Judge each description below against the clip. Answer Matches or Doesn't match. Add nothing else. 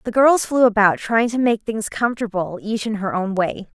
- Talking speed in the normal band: Doesn't match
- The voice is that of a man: Doesn't match